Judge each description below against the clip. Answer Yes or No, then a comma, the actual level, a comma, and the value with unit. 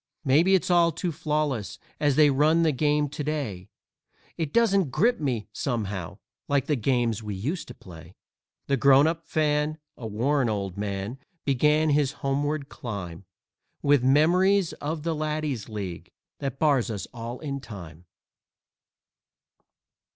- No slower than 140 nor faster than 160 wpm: Yes, average, 145 wpm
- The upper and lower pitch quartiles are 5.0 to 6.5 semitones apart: Yes, average, 5.3 semitones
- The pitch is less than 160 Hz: Yes, medium, 140 Hz